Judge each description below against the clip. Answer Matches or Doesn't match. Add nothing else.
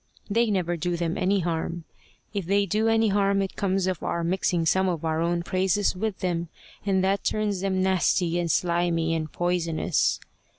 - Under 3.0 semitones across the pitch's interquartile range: Matches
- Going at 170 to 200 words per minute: Matches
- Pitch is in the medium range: Matches